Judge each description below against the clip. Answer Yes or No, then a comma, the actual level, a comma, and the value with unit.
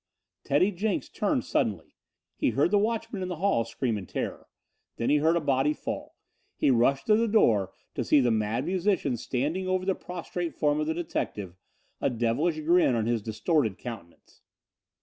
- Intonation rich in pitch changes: Yes, wide, 7.4 semitones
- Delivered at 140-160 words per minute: No, average, 180 wpm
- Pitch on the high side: No, medium, 150 Hz